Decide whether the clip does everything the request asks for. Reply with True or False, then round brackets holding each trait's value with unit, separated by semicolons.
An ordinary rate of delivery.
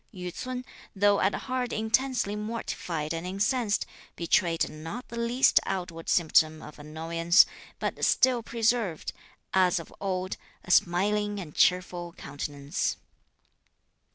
False (120 wpm)